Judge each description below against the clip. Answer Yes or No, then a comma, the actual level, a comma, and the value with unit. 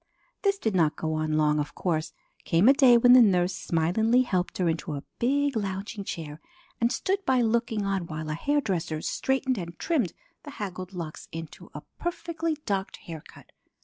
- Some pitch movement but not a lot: No, wide, 7.6 semitones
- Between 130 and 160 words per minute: No, average, 180 wpm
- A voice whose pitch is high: Yes, high, 195 Hz